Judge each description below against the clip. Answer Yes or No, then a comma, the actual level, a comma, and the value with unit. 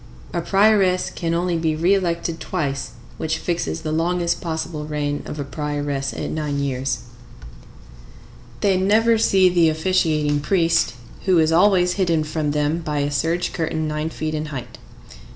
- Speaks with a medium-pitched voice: Yes, medium, 160 Hz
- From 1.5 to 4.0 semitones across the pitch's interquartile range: Yes, average, 3.0 semitones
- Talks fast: No, average, 155 wpm